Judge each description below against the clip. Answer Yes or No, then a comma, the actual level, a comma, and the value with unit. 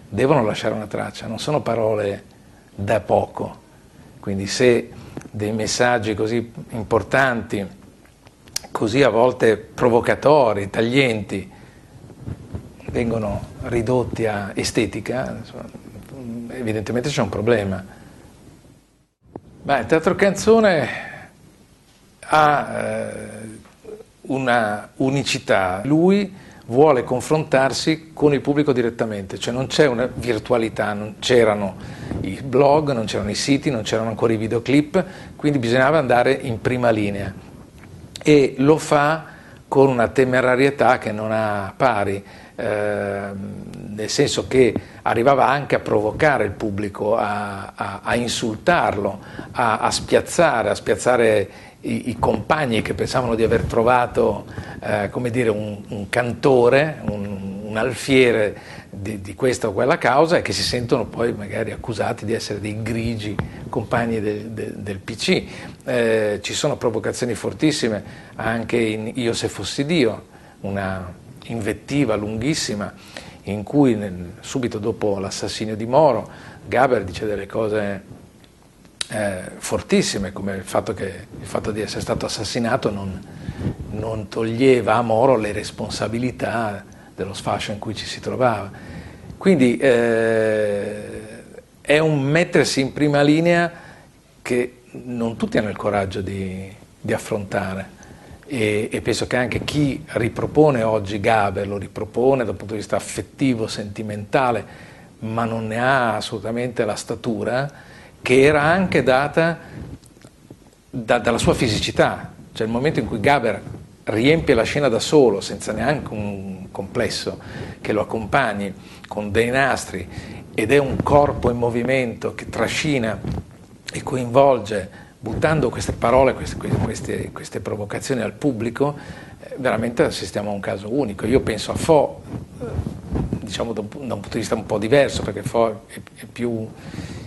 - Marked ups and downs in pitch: No, average, 4.0 semitones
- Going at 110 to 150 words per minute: Yes, average, 130 wpm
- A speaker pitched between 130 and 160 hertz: No, low, 115 Hz